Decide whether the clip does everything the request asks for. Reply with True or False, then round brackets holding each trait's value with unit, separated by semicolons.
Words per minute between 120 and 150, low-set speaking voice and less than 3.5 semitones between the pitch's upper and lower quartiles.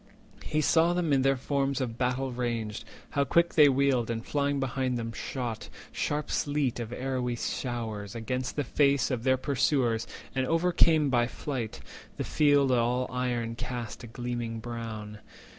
False (160 wpm; 125 Hz; 3.0 semitones)